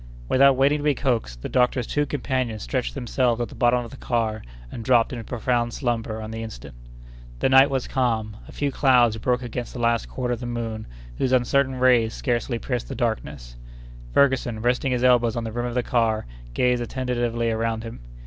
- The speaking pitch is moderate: No, low, 120 Hz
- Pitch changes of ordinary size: No, narrow, 2.1 semitones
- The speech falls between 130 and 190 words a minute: No, average, 200 wpm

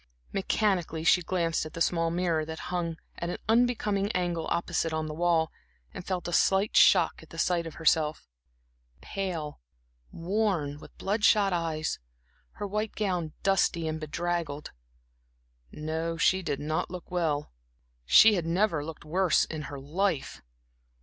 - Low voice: No, medium, 170 Hz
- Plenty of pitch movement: No, average, 3.1 semitones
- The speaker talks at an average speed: Yes, average, 150 wpm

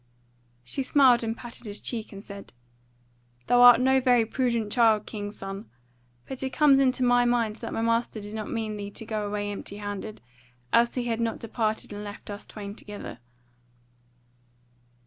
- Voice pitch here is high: Yes, high, 225 Hz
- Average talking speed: Yes, average, 175 wpm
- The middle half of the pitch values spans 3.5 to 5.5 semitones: No, average, 2.9 semitones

